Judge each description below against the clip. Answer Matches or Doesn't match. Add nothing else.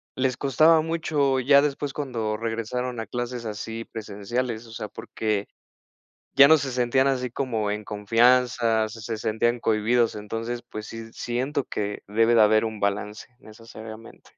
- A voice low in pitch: Matches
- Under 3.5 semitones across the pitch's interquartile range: Matches